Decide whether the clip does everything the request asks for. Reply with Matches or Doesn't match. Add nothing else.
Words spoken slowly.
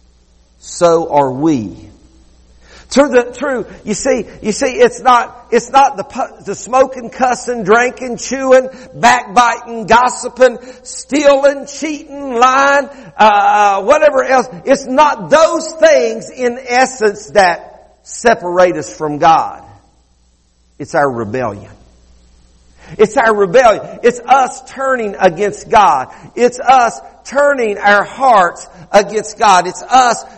Matches